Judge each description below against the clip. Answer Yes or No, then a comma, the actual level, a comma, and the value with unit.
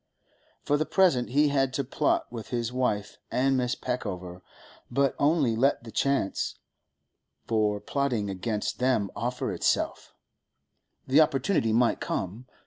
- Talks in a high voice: No, low, 125 Hz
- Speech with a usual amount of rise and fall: Yes, average, 3.9 semitones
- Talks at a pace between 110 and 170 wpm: Yes, slow, 135 wpm